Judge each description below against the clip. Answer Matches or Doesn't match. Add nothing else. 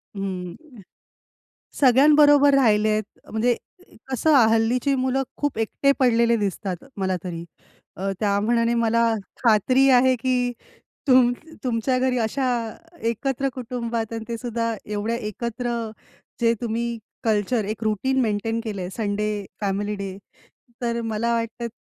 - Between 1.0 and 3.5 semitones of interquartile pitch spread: Matches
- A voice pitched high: Matches